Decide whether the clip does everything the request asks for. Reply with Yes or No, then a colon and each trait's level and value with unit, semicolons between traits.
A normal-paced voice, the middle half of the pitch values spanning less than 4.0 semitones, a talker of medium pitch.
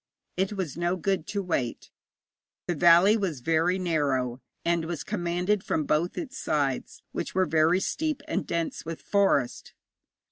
Yes: average, 150 wpm; average, 3.6 semitones; medium, 175 Hz